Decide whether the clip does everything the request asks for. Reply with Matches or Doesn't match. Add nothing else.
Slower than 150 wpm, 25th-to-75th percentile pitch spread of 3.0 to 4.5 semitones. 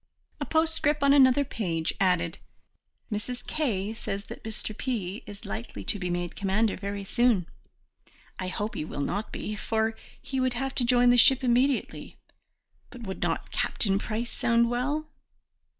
Doesn't match